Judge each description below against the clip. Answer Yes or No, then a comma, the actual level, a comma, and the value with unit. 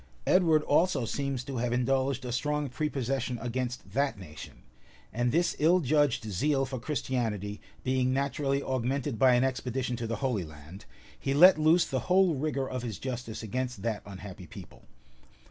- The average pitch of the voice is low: Yes, low, 130 Hz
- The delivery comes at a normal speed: Yes, average, 165 wpm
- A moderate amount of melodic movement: Yes, average, 3.2 semitones